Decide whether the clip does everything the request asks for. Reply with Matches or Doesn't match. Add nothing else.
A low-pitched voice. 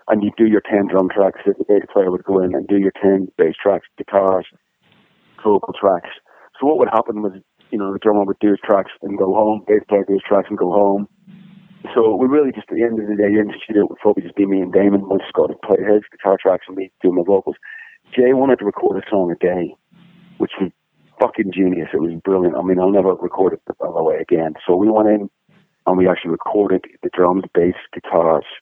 Matches